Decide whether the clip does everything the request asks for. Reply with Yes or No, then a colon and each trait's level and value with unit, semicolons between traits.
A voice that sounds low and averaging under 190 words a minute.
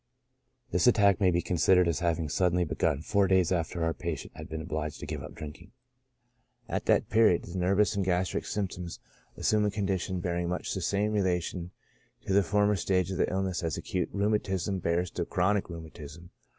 No: very low, 90 Hz; average, 195 wpm